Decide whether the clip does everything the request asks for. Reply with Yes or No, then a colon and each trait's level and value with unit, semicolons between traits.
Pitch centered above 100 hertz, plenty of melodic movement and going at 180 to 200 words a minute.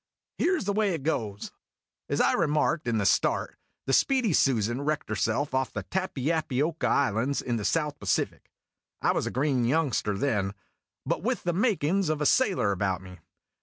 Yes: medium, 140 Hz; wide, 6.6 semitones; average, 185 wpm